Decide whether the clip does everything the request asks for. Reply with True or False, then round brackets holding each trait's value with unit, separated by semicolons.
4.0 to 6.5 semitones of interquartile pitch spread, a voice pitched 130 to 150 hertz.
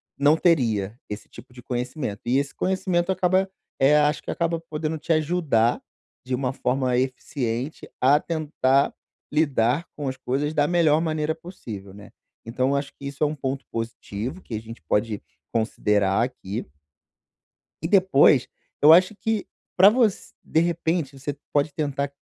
True (4.7 semitones; 140 Hz)